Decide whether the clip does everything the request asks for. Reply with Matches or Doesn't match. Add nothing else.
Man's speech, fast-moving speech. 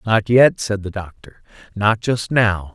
Doesn't match